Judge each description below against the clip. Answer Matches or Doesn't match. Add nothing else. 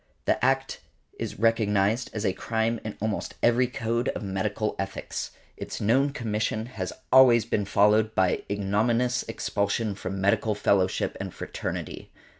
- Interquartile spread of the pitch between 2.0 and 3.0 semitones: Matches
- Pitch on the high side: Doesn't match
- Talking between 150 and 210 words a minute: Doesn't match